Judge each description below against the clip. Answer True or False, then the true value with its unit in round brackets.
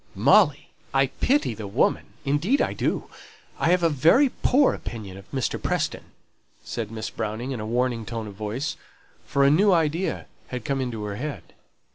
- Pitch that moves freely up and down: True (6.3 semitones)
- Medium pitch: False (130 Hz)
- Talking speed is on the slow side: False (175 wpm)